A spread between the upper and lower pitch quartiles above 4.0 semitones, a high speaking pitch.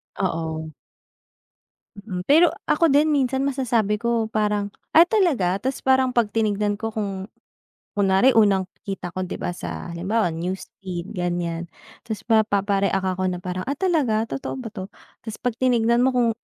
Yes: average, 4.8 semitones; high, 210 Hz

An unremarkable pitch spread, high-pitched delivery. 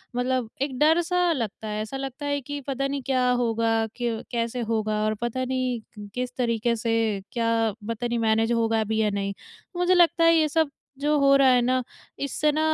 Yes: average, 3.7 semitones; very high, 250 Hz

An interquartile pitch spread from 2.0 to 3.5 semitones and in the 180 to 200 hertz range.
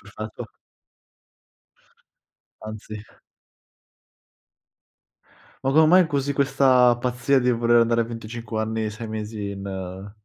No: average, 2.7 semitones; low, 115 Hz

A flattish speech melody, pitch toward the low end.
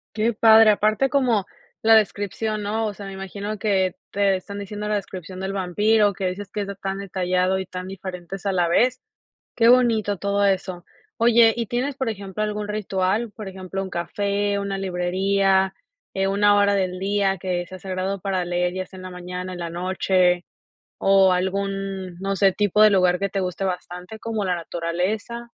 No: narrow, 2.0 semitones; high, 195 Hz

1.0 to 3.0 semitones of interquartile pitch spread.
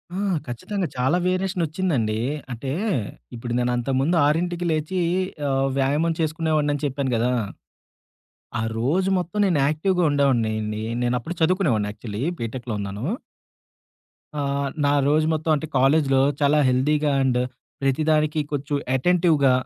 No: average, 4.1 semitones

